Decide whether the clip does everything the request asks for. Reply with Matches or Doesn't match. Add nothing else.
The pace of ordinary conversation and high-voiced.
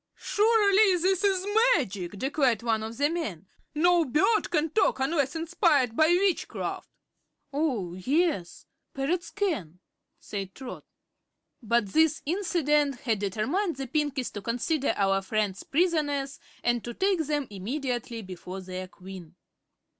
Doesn't match